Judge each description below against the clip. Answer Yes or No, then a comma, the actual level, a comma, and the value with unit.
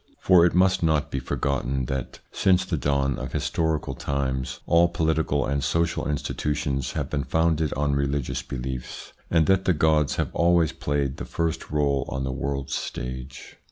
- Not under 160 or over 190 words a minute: Yes, average, 165 wpm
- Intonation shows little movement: No, average, 3.2 semitones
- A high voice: No, very low, 70 Hz